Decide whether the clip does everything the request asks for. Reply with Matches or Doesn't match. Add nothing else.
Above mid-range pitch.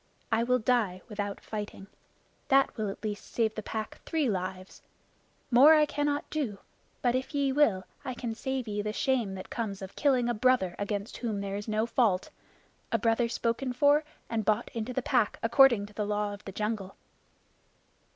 Matches